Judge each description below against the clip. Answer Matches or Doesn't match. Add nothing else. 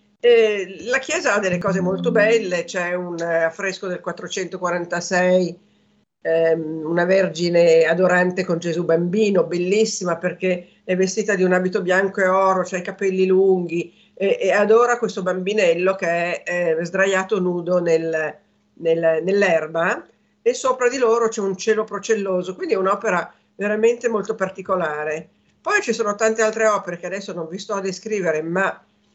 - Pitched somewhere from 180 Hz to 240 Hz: Matches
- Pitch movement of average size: Matches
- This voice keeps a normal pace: Matches